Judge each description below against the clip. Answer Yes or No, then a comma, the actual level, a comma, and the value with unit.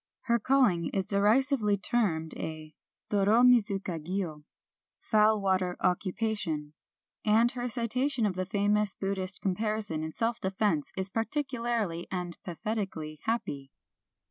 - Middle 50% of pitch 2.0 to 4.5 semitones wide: Yes, average, 4.2 semitones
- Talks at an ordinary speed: No, slow, 120 wpm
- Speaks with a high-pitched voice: Yes, high, 205 Hz